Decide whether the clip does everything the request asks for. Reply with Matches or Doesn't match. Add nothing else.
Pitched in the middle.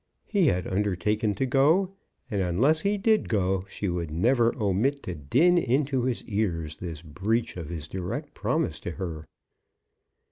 Doesn't match